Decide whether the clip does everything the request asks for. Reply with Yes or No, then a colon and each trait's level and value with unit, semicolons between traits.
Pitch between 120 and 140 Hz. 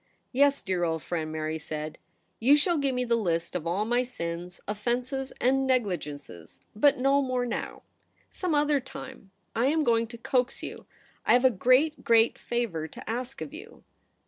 No: high, 240 Hz